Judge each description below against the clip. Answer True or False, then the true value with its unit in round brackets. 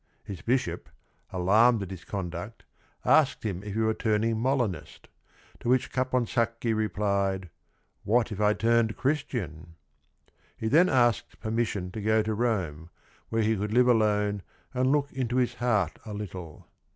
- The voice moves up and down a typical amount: True (3.6 semitones)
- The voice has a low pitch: True (110 Hz)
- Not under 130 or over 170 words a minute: True (150 wpm)